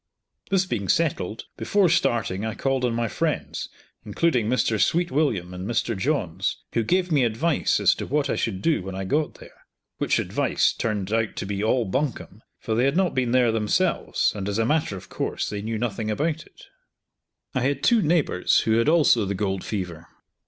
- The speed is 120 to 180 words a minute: No, average, 195 wpm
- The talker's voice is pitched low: Yes, low, 115 Hz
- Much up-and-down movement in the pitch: Yes, wide, 6.3 semitones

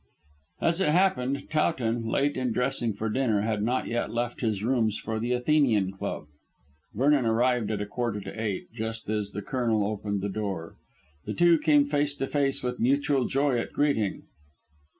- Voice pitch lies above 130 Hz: No, low, 120 Hz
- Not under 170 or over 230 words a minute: Yes, average, 175 wpm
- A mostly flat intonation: No, average, 4.3 semitones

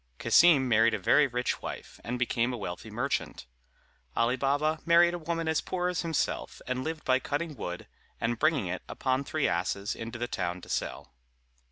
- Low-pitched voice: Yes, low, 130 Hz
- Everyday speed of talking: Yes, average, 185 wpm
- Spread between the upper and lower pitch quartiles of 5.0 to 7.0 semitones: Yes, wide, 5.5 semitones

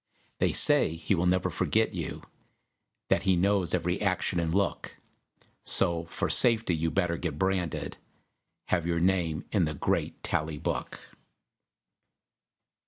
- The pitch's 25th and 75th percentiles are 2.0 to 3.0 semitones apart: Yes, narrow, 2.4 semitones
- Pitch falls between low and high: No, very low, 90 Hz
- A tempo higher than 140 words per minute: No, slow, 135 wpm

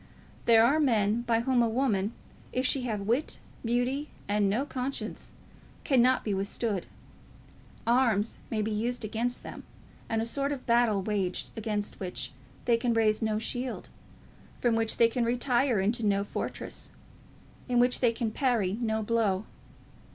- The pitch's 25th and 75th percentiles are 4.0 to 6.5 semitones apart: No, narrow, 2.6 semitones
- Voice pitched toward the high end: Yes, high, 230 Hz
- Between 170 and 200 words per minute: No, average, 155 wpm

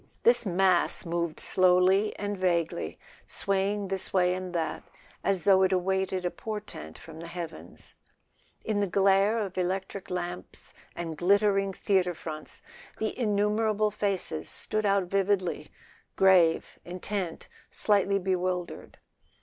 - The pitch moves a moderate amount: No, narrow, 2.1 semitones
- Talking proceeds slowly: Yes, slow, 125 wpm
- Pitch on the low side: No, high, 190 Hz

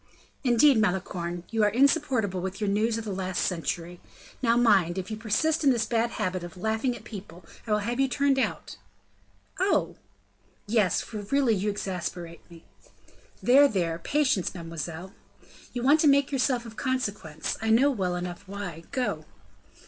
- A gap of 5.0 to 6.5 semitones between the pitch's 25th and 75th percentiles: Yes, wide, 5.5 semitones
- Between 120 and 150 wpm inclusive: No, average, 165 wpm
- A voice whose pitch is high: Yes, high, 210 Hz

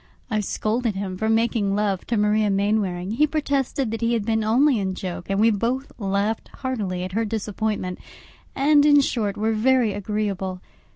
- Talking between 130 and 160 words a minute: No, average, 175 wpm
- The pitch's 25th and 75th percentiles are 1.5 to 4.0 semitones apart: Yes, average, 2.9 semitones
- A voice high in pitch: Yes, high, 215 Hz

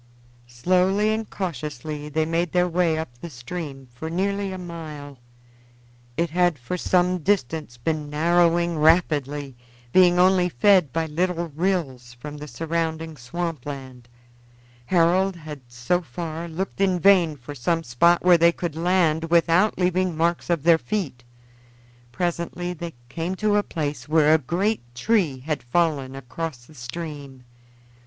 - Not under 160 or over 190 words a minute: No, average, 145 wpm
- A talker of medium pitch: Yes, medium, 165 Hz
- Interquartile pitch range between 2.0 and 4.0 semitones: Yes, average, 3.4 semitones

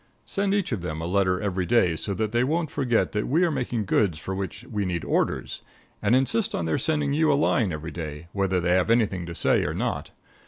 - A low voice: Yes, low, 105 Hz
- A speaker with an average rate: No, fast, 235 wpm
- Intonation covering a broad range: Yes, wide, 6.9 semitones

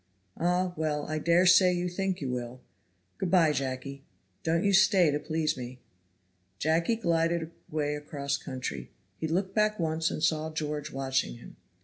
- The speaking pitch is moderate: Yes, medium, 160 Hz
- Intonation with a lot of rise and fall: No, average, 3.5 semitones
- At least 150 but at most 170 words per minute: Yes, average, 155 wpm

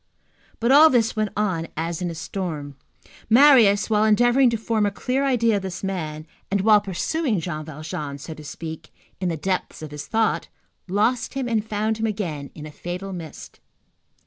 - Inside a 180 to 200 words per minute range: Yes, average, 185 wpm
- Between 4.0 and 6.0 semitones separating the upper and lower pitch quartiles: Yes, wide, 5.5 semitones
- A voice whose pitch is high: Yes, high, 200 Hz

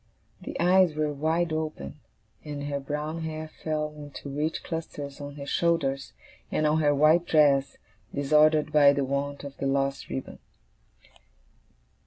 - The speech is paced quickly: No, average, 150 wpm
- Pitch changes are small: Yes, narrow, 1.8 semitones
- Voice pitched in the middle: Yes, medium, 150 Hz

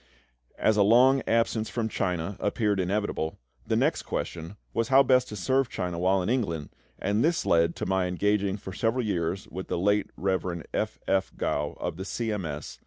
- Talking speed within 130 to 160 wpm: No, average, 190 wpm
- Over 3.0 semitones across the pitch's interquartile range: Yes, average, 3.8 semitones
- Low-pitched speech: Yes, low, 100 Hz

